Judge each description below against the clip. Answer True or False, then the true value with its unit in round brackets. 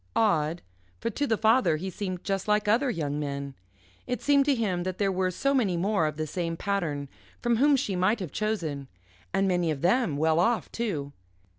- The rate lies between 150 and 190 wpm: False (200 wpm)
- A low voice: False (190 Hz)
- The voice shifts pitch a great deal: True (5.7 semitones)